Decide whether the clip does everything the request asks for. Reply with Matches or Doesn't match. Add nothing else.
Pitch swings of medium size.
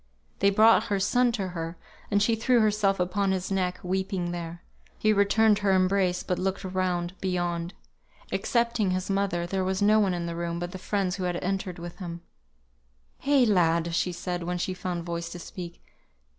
Doesn't match